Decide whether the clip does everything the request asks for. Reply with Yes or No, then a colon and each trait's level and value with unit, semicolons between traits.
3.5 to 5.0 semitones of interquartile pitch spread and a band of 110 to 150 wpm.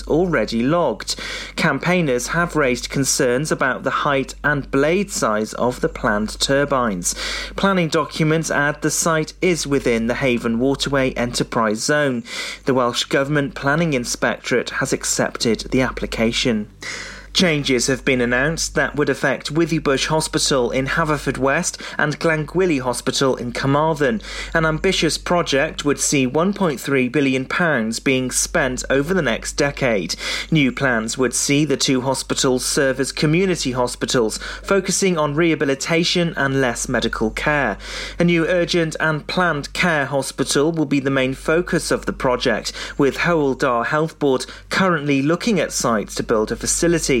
Yes: average, 4.0 semitones; average, 140 wpm